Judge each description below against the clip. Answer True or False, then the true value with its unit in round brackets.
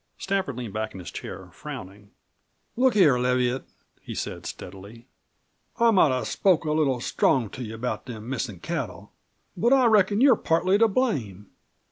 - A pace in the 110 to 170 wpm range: True (165 wpm)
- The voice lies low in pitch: True (130 Hz)